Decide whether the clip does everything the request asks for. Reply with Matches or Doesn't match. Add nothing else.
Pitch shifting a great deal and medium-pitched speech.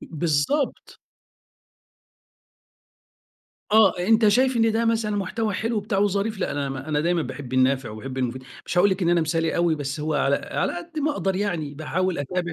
Matches